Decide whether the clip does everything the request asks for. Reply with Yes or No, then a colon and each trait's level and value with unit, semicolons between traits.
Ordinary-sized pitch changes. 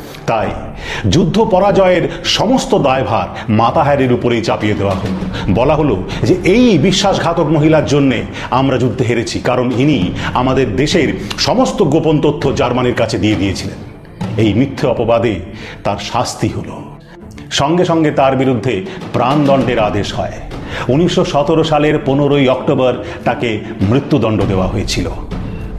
No: wide, 5.7 semitones